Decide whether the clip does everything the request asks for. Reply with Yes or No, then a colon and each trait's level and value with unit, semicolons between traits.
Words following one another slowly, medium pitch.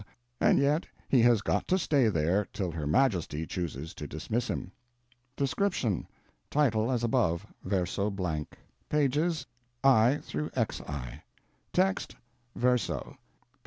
No: slow, 120 wpm; low, 110 Hz